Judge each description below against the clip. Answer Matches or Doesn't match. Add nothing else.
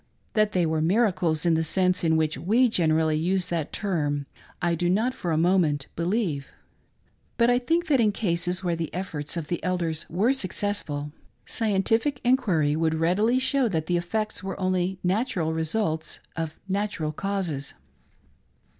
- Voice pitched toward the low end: Doesn't match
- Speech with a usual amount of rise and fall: Matches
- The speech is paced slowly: Doesn't match